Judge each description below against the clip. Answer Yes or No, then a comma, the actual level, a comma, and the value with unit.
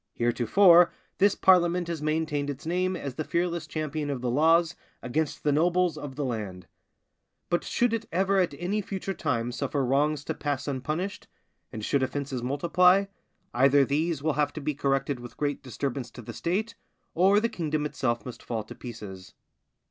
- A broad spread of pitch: No, average, 4.8 semitones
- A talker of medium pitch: Yes, medium, 150 Hz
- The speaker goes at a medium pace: Yes, average, 175 wpm